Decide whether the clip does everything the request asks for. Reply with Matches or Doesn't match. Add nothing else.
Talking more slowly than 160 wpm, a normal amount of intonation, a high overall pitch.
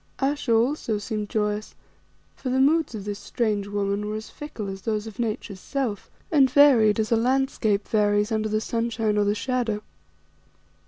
Doesn't match